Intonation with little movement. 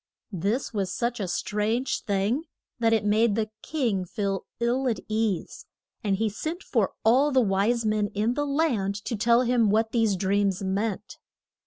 No: average, 3.1 semitones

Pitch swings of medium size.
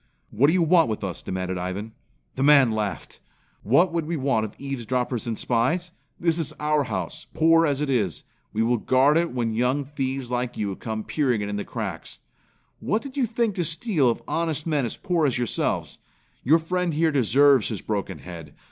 No: wide, 6.4 semitones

